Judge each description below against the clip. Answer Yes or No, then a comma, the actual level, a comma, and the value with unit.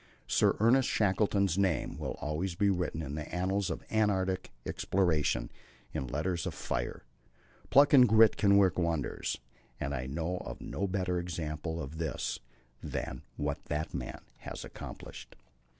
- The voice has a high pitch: No, very low, 90 Hz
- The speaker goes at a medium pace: Yes, average, 150 wpm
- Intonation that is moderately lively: Yes, average, 4.3 semitones